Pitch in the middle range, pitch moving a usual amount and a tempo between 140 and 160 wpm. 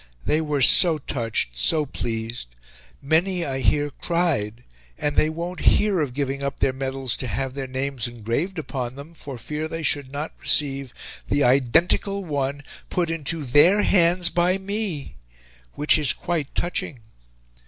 Yes: medium, 145 Hz; average, 4.2 semitones; average, 155 wpm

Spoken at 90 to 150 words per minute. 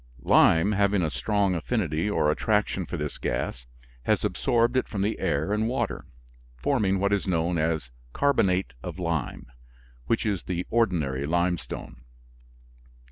Yes: average, 140 wpm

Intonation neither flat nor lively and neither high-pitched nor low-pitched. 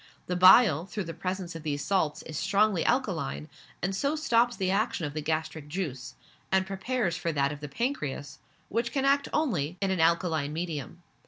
Yes: average, 4.8 semitones; medium, 175 Hz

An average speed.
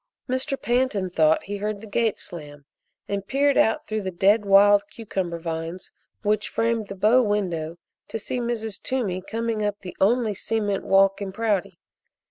Yes: average, 165 wpm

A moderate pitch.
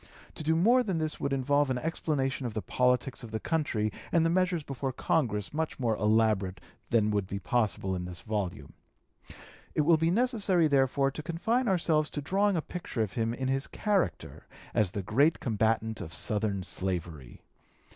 No: low, 130 Hz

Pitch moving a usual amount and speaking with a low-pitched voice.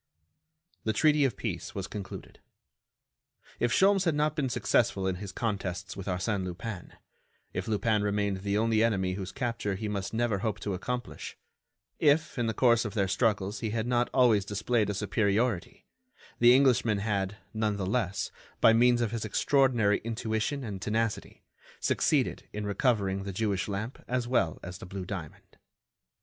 Yes: average, 3.4 semitones; low, 110 Hz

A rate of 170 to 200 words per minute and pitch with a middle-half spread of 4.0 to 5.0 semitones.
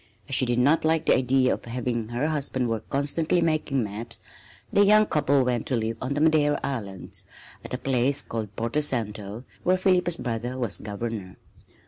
Yes: average, 180 wpm; average, 4.5 semitones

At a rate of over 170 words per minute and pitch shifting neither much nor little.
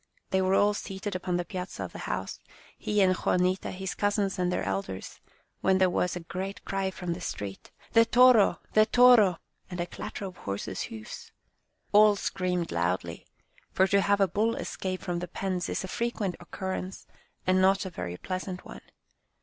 No: average, 190 wpm; narrow, 2.0 semitones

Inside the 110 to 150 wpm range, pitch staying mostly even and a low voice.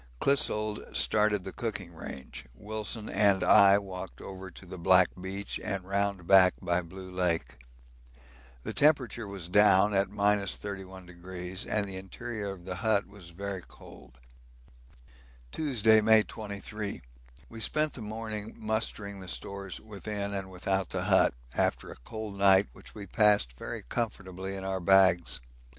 Yes: average, 145 wpm; narrow, 2.2 semitones; low, 100 Hz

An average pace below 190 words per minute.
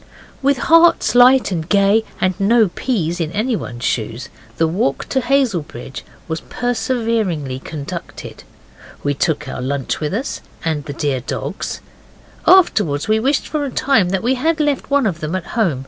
Yes: average, 165 wpm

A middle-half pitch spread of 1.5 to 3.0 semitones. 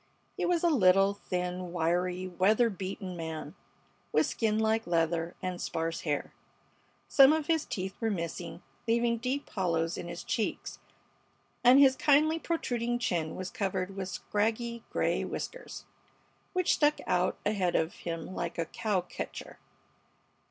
No: average, 5.1 semitones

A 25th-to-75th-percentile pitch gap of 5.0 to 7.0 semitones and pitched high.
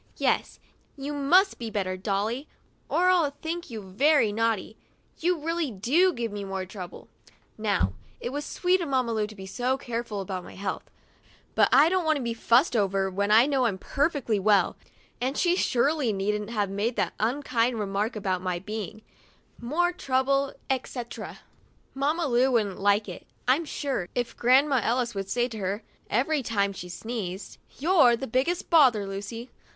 Yes: wide, 5.5 semitones; high, 235 Hz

